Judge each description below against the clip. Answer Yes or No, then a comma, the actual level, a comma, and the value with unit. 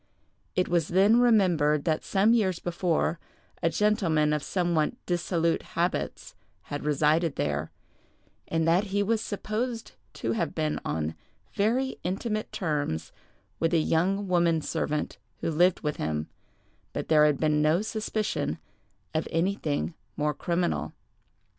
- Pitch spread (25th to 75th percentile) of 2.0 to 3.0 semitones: No, average, 4.5 semitones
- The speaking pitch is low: No, medium, 170 Hz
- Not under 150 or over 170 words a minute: No, slow, 135 wpm